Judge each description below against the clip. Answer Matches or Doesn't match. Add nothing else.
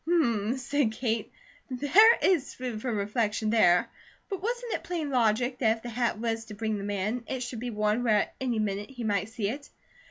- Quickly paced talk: Matches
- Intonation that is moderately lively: Matches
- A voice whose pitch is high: Matches